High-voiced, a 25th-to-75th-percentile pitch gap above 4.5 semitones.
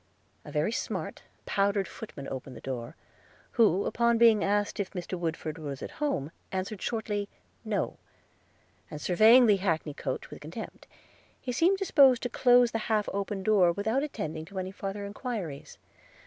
Yes: high, 200 Hz; average, 5.0 semitones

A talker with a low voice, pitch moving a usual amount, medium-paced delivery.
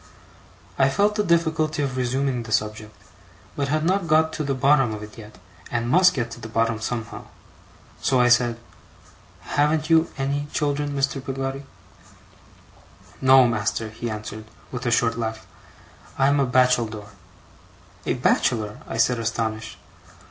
Yes: low, 125 Hz; average, 4.1 semitones; average, 150 wpm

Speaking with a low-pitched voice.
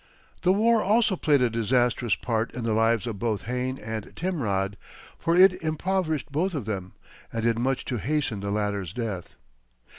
Yes: low, 120 Hz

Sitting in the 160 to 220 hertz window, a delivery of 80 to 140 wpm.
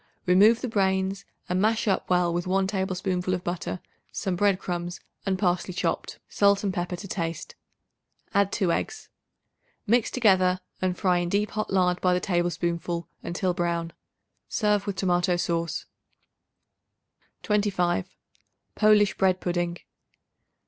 Yes: medium, 185 Hz; slow, 135 wpm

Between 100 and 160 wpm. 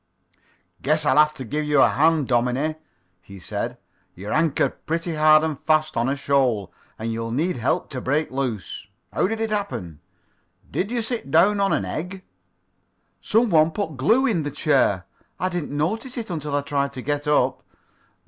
No: average, 185 wpm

